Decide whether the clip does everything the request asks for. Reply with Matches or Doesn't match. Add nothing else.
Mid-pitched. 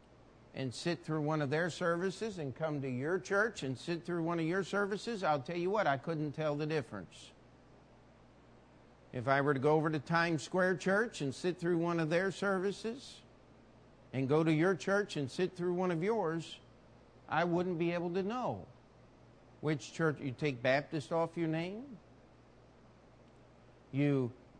Matches